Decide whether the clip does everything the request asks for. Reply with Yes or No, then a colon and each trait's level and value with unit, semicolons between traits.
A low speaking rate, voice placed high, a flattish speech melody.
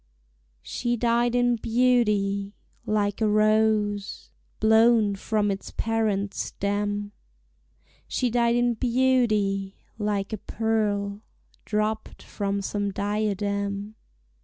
Yes: slow, 95 wpm; high, 210 Hz; narrow, 2.0 semitones